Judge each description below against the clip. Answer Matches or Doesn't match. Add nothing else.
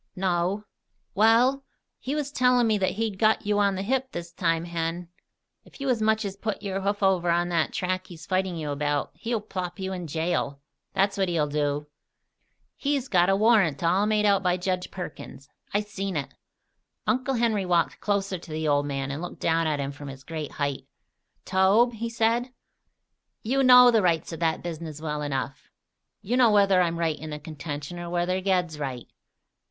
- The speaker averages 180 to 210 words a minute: Matches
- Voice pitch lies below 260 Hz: Matches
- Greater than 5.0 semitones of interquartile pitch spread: Doesn't match